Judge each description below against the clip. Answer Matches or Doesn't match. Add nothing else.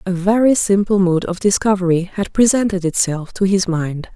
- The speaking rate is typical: Matches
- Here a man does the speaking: Doesn't match